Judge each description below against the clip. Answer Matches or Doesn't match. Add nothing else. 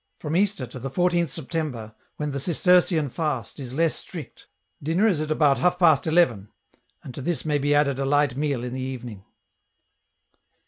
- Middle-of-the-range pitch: Matches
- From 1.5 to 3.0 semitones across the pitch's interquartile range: Doesn't match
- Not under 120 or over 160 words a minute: Doesn't match